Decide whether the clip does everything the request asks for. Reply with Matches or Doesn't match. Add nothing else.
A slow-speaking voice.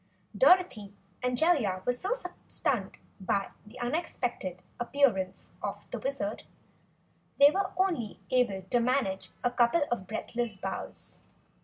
Matches